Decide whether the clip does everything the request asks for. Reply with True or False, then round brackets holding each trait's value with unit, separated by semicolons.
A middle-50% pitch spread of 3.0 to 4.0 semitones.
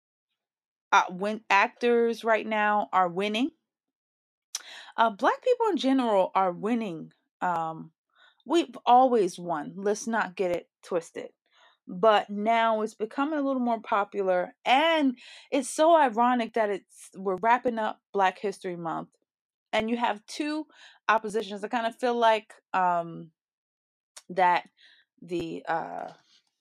False (4.4 semitones)